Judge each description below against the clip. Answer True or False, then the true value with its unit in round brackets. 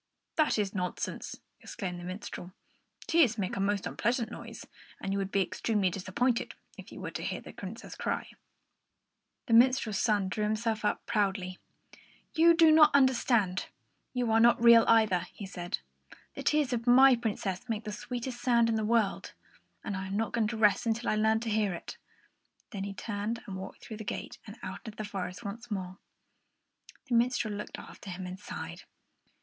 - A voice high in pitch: True (215 Hz)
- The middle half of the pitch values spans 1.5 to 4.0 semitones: True (3.3 semitones)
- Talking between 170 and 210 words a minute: True (190 wpm)